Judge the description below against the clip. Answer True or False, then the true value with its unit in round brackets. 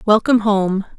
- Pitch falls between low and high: False (210 Hz)